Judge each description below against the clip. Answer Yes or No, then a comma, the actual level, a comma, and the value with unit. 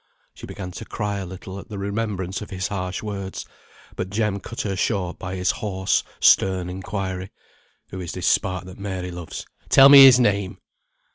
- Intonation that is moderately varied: No, narrow, 1.8 semitones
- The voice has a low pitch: Yes, very low, 95 Hz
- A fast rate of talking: No, average, 185 wpm